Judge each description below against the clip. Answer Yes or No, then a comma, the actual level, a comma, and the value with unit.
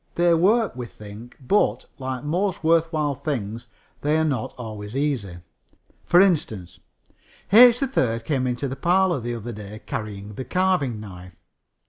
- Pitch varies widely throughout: Yes, wide, 7.6 semitones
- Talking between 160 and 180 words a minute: No, average, 150 wpm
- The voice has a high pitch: No, low, 130 Hz